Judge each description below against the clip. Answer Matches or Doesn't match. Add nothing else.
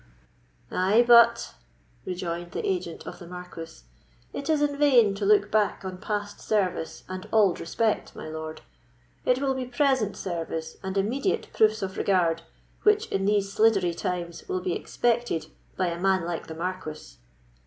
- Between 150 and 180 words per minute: Matches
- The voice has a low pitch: Doesn't match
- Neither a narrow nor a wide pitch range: Matches